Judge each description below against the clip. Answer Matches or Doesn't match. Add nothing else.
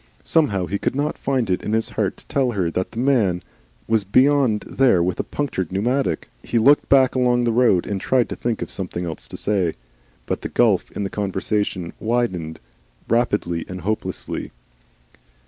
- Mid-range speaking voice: Doesn't match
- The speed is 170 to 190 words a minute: Matches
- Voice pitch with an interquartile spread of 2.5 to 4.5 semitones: Doesn't match